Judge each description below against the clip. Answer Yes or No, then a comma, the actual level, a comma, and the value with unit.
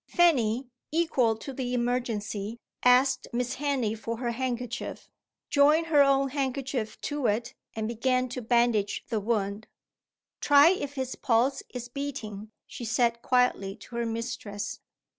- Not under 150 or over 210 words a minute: No, average, 140 wpm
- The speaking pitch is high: Yes, high, 245 Hz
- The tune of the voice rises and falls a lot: No, average, 3.2 semitones